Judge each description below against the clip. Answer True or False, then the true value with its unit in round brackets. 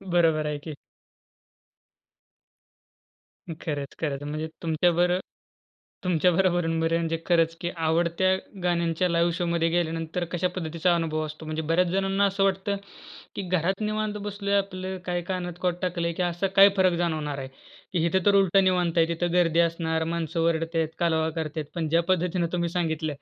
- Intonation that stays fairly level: True (2.0 semitones)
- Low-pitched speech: False (170 Hz)